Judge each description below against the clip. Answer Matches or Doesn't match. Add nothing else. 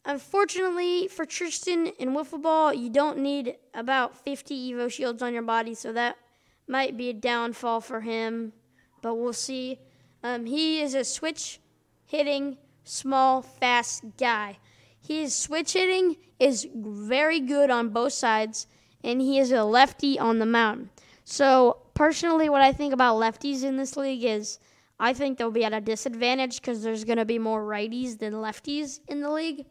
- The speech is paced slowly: Doesn't match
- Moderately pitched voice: Doesn't match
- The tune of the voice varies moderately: Matches